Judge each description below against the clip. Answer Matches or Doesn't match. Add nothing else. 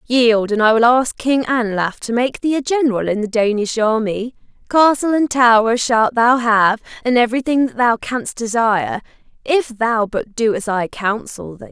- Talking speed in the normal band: Matches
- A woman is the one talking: Matches